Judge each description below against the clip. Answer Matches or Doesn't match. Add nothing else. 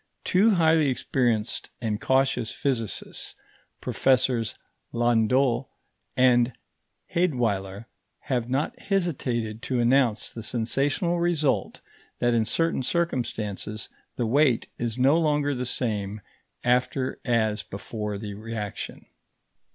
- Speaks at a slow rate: Matches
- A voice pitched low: Matches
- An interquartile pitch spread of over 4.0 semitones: Doesn't match